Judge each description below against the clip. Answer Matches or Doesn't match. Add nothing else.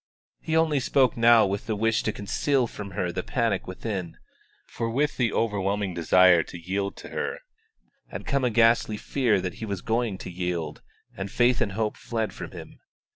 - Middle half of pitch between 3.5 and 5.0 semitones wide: Matches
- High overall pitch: Doesn't match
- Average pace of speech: Matches